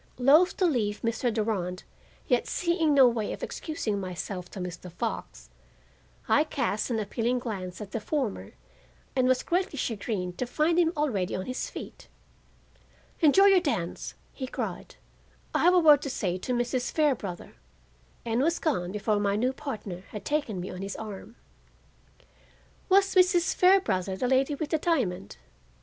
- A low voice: No, high, 245 Hz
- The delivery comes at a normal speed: Yes, average, 160 wpm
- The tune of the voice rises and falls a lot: Yes, wide, 7.2 semitones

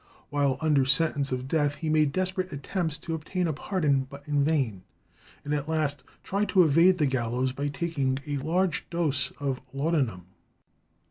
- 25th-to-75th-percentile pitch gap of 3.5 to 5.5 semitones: No, average, 3.1 semitones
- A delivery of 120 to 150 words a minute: No, average, 170 wpm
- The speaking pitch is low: No, medium, 145 Hz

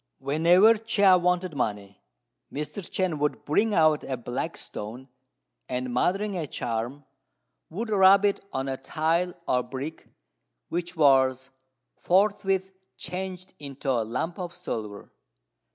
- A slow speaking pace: Yes, slow, 130 wpm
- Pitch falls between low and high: Yes, medium, 160 Hz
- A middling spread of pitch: No, wide, 6.0 semitones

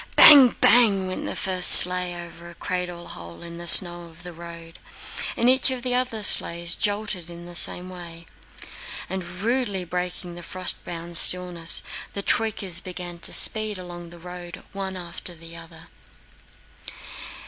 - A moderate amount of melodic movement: No, narrow, 2.0 semitones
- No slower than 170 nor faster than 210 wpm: No, average, 160 wpm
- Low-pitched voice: No, medium, 180 Hz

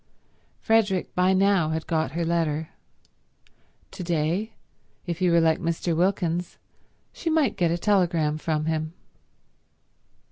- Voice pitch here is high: No, medium, 170 Hz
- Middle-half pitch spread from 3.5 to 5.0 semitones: No, average, 2.7 semitones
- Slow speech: Yes, slow, 130 wpm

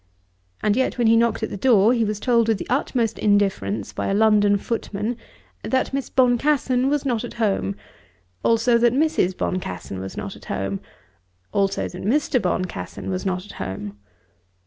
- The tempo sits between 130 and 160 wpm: No, average, 170 wpm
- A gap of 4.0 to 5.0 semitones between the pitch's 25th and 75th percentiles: Yes, average, 4.6 semitones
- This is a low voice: No, high, 220 Hz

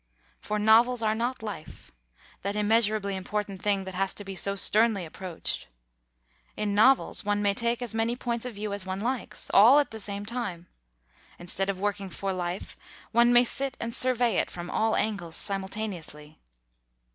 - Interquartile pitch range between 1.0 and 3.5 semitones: Yes, average, 3.1 semitones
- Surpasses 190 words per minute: No, average, 170 wpm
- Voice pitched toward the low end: No, high, 210 Hz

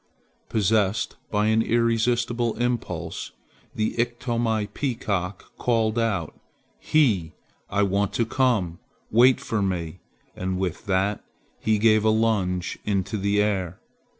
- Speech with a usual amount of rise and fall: Yes, average, 3.3 semitones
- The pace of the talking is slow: Yes, slow, 120 wpm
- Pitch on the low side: Yes, low, 110 Hz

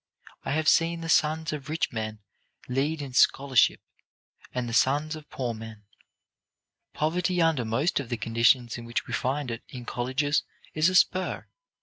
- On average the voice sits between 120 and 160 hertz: Yes, medium, 140 Hz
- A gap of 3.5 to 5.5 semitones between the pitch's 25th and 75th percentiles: Yes, average, 4.7 semitones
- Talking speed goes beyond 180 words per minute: No, average, 165 wpm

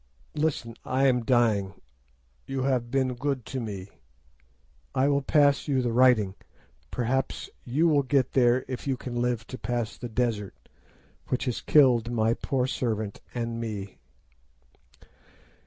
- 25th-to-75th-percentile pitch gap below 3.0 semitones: Yes, narrow, 2.5 semitones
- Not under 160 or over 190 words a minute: No, average, 140 wpm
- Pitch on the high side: No, low, 125 Hz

